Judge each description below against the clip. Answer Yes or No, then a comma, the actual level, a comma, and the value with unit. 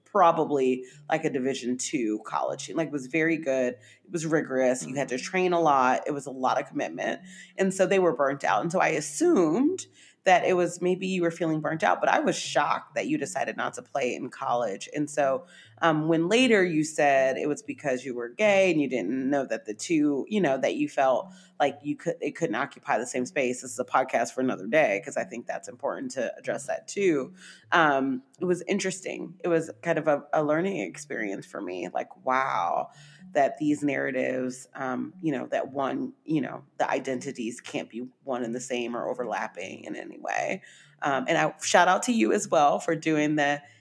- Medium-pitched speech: Yes, medium, 150 Hz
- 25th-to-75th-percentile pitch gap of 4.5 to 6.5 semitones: Yes, average, 5.2 semitones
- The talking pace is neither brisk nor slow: No, fast, 215 wpm